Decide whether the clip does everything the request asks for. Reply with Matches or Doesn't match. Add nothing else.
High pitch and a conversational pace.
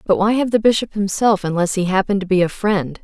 Doesn't match